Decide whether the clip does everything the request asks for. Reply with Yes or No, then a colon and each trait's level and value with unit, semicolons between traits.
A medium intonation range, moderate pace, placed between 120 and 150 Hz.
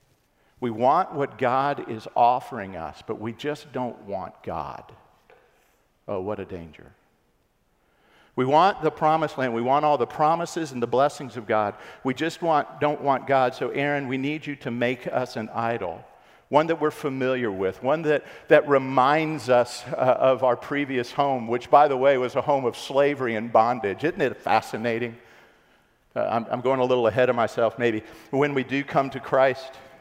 Yes: average, 3.3 semitones; average, 190 wpm; low, 130 Hz